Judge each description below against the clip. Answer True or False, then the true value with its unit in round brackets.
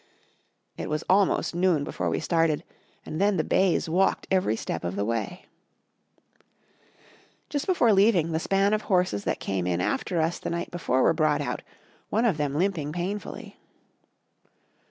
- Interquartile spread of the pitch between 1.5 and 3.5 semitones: False (4.7 semitones)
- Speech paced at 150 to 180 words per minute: True (160 wpm)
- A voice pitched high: False (170 Hz)